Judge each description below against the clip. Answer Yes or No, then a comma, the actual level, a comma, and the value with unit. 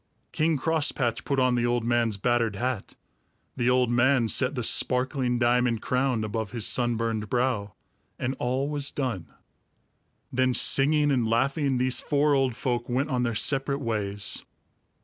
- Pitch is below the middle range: Yes, low, 125 Hz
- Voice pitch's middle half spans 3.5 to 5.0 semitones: No, narrow, 2.5 semitones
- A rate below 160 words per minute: Yes, average, 150 wpm